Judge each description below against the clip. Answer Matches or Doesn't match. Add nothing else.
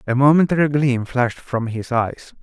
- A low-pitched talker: Matches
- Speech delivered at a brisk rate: Doesn't match